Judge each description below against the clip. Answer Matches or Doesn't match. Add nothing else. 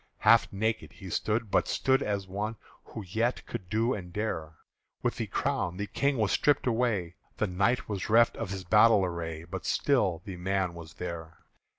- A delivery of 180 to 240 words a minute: Matches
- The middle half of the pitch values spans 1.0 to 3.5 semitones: Doesn't match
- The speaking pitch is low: Matches